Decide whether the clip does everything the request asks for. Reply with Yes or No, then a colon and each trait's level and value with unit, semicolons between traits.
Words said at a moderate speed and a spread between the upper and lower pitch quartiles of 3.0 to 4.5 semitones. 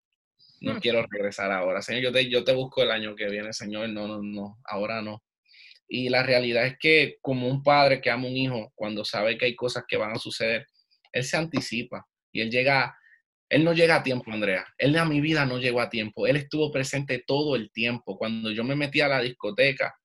No: fast, 225 wpm; average, 3.4 semitones